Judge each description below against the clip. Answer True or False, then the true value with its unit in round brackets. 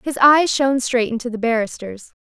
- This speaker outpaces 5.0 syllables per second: True (5.4 syllables/s)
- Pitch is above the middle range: True (245 Hz)